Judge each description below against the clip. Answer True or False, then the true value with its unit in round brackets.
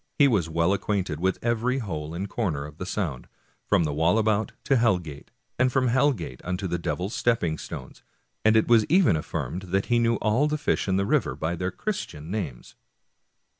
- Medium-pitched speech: False (100 Hz)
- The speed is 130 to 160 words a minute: False (205 wpm)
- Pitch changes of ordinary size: False (5.9 semitones)